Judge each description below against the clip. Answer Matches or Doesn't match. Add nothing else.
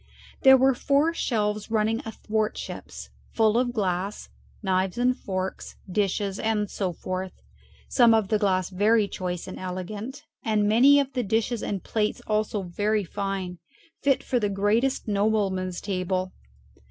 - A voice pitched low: Doesn't match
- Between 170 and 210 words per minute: Doesn't match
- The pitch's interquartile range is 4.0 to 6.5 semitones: Doesn't match